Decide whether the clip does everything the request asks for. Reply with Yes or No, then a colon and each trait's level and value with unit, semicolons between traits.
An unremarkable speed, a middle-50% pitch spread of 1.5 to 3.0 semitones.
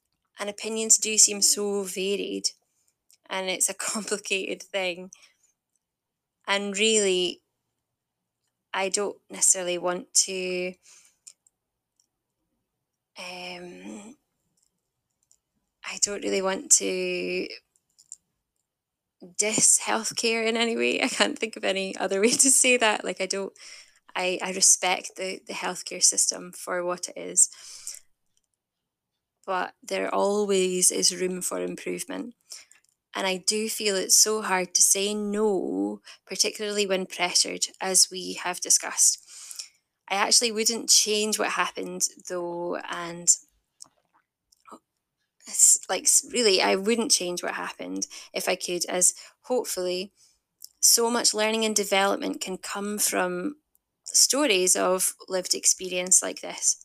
No: slow, 115 wpm; average, 2.7 semitones